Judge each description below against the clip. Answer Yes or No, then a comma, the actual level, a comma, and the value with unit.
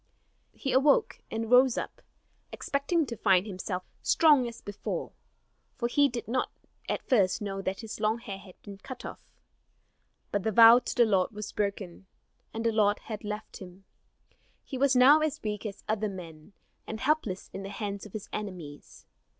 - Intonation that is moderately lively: Yes, average, 4.2 semitones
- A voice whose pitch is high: Yes, high, 215 Hz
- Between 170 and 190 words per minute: Yes, average, 175 wpm